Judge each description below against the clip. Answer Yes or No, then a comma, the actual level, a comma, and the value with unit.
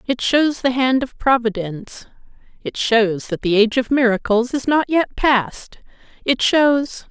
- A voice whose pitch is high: Yes, high, 245 Hz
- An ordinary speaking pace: Yes, average, 160 wpm